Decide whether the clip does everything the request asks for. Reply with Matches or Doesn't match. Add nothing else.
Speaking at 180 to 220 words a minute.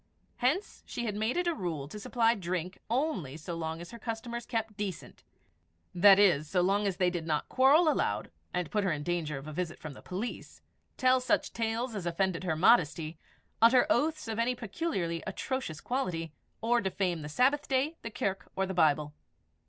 Matches